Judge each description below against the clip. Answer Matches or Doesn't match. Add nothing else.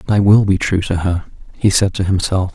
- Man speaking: Matches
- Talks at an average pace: Doesn't match